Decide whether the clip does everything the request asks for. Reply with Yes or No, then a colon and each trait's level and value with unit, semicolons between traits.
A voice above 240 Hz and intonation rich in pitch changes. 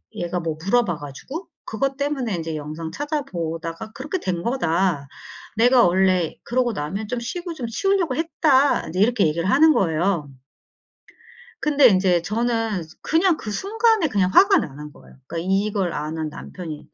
No: high, 205 Hz; wide, 8.5 semitones